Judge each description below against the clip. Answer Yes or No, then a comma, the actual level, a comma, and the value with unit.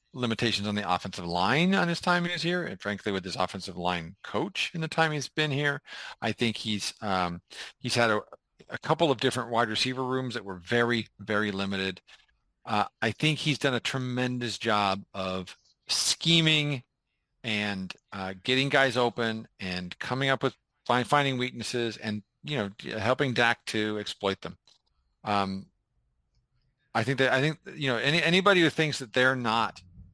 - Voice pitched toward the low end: Yes, low, 120 Hz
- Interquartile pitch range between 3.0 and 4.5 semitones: No, average, 5.2 semitones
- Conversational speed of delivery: Yes, average, 175 wpm